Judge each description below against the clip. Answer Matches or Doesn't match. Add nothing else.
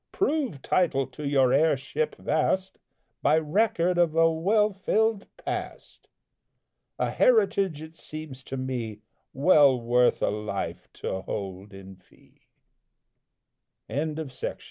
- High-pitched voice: Doesn't match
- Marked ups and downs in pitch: Matches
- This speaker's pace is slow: Matches